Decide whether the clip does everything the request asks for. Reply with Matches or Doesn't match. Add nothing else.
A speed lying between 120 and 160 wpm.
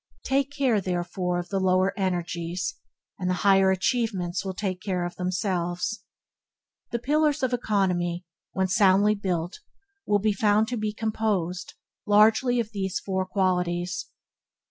Matches